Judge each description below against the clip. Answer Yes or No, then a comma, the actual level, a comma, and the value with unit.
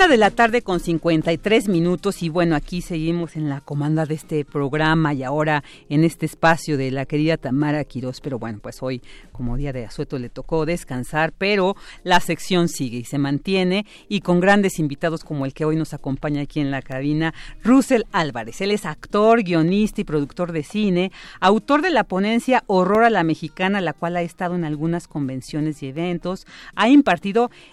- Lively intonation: No, average, 4.4 semitones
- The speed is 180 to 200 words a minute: Yes, fast, 190 wpm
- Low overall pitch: No, medium, 165 Hz